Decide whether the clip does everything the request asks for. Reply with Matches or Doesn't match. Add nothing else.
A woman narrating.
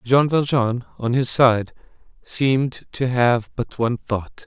Doesn't match